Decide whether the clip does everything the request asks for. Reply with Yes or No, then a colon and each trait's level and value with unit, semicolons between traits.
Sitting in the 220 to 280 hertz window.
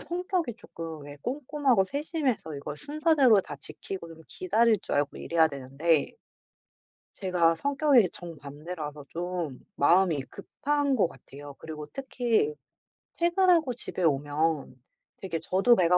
No: medium, 185 Hz